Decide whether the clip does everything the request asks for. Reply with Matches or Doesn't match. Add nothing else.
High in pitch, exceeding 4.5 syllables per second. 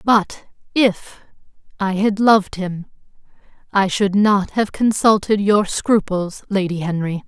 Doesn't match